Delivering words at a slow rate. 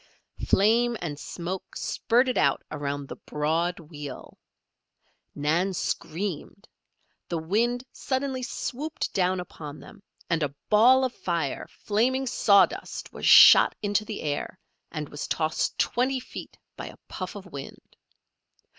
Yes: slow, 130 wpm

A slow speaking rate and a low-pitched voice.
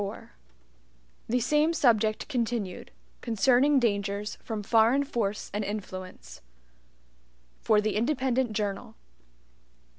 No: slow, 95 wpm; high, 220 Hz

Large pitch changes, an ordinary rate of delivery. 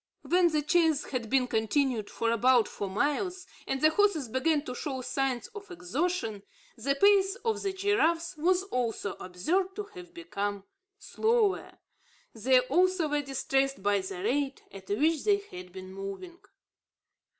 Yes: wide, 7.9 semitones; average, 150 wpm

